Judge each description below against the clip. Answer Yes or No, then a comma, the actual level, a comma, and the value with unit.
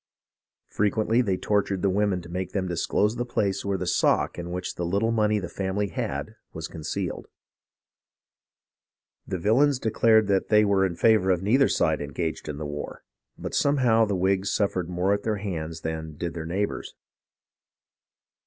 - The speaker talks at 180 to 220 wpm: No, average, 165 wpm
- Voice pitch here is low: Yes, very low, 95 Hz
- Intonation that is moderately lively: Yes, average, 3.5 semitones